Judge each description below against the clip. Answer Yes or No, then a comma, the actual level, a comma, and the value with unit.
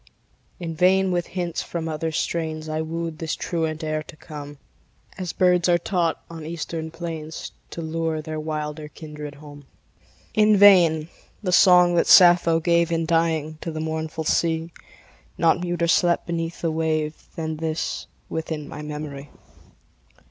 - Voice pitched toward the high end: No, medium, 160 Hz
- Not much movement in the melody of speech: Yes, narrow, 1.6 semitones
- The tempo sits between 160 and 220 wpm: No, average, 150 wpm